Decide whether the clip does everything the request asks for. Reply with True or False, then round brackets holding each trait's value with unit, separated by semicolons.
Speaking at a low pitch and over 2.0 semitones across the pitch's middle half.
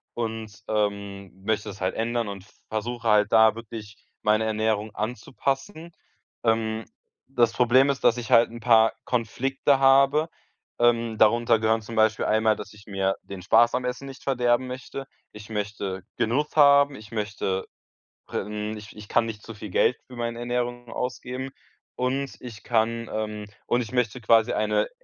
True (115 Hz; 2.6 semitones)